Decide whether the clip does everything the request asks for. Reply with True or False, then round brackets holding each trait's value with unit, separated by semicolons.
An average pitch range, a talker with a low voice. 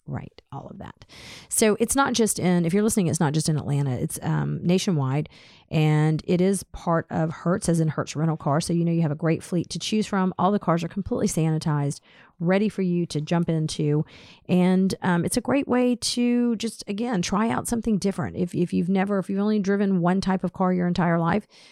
False (4.0 semitones; 180 Hz)